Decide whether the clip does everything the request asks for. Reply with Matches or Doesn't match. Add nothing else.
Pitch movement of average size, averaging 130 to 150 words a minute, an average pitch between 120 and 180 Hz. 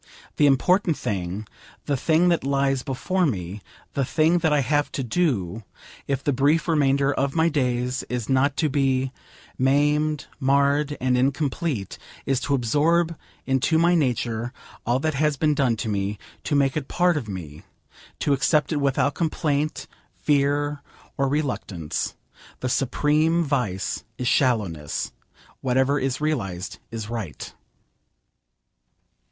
Matches